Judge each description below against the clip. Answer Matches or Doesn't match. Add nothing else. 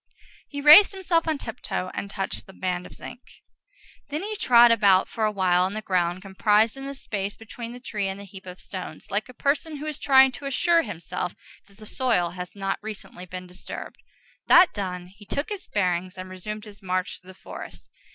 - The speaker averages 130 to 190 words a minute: Doesn't match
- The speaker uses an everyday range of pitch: Doesn't match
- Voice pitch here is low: Doesn't match